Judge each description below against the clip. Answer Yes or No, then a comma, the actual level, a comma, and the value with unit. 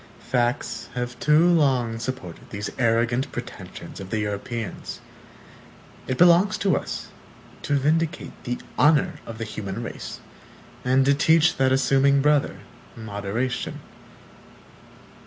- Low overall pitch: Yes, low, 130 Hz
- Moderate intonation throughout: Yes, average, 4.4 semitones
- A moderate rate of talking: No, slow, 120 wpm